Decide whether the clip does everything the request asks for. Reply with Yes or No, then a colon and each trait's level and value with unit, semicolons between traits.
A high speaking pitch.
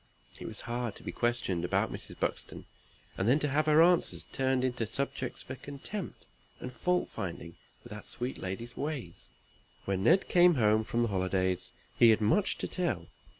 No: low, 120 Hz